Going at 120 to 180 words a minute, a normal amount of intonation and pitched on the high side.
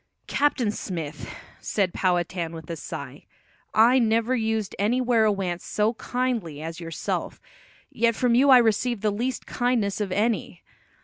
Yes: average, 140 wpm; average, 4.7 semitones; high, 220 Hz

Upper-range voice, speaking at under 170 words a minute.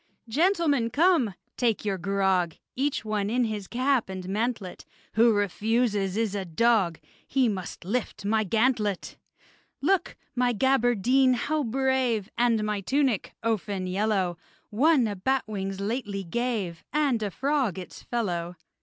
Yes: high, 220 Hz; slow, 135 wpm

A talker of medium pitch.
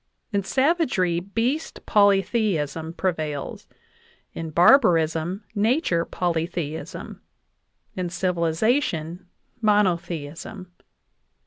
Yes: medium, 180 Hz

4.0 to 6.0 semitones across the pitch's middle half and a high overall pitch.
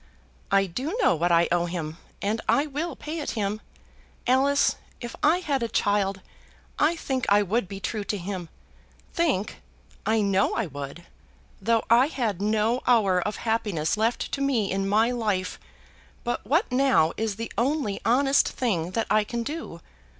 Yes: average, 5.0 semitones; high, 220 Hz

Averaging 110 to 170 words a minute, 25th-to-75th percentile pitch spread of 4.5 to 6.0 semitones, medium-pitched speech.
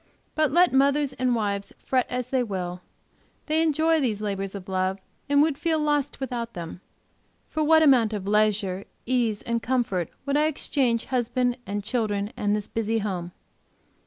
No: average, 165 wpm; wide, 5.5 semitones; high, 235 Hz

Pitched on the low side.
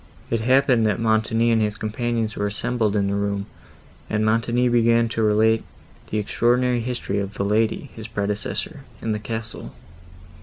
Yes: low, 110 Hz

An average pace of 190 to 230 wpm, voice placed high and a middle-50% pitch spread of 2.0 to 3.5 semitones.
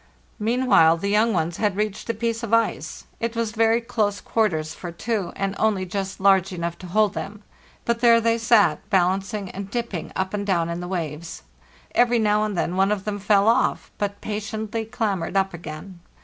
Yes: average, 195 wpm; high, 205 Hz; average, 3.2 semitones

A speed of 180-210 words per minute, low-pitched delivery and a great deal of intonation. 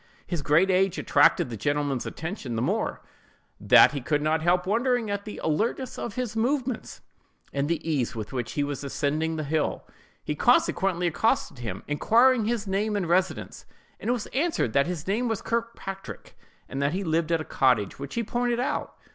No: average, 185 wpm; medium, 175 Hz; wide, 7.4 semitones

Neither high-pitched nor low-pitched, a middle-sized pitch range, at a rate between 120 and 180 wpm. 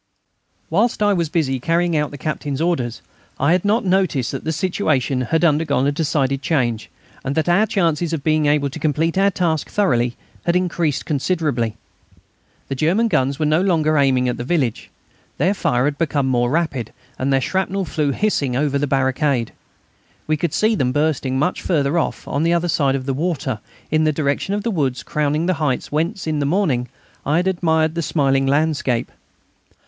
No: medium, 150 Hz; average, 4.0 semitones; average, 190 wpm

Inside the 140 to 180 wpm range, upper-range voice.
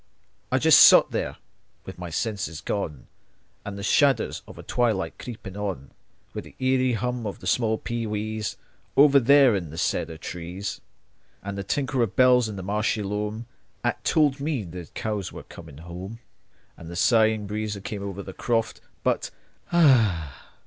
No: average, 170 wpm; low, 105 Hz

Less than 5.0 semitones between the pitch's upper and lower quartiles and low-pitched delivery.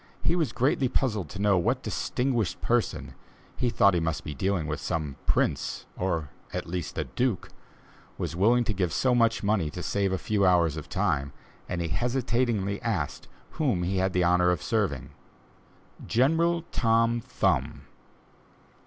No: wide, 5.6 semitones; low, 100 Hz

